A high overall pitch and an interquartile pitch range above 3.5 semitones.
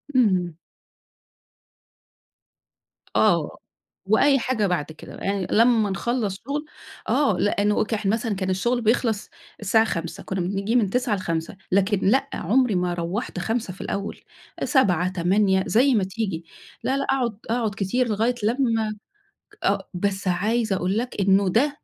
Yes: high, 205 Hz; average, 3.9 semitones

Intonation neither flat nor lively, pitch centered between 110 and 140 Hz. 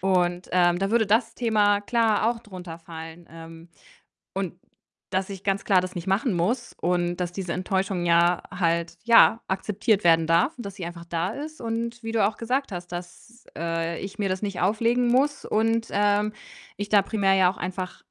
No: average, 4.1 semitones; high, 195 Hz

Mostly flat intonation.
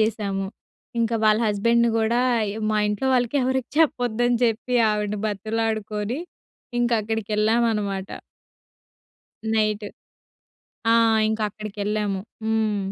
Yes: narrow, 1.8 semitones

